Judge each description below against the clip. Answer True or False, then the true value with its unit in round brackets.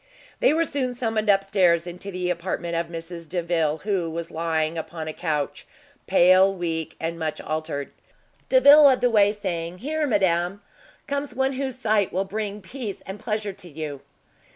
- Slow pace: False (165 wpm)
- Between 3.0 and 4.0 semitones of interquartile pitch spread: False (4.5 semitones)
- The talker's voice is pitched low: False (185 Hz)